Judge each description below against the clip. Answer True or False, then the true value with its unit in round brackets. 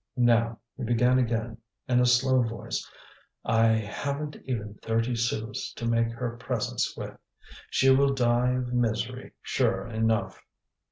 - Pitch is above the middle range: False (120 Hz)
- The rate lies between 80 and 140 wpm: True (135 wpm)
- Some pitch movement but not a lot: False (1.7 semitones)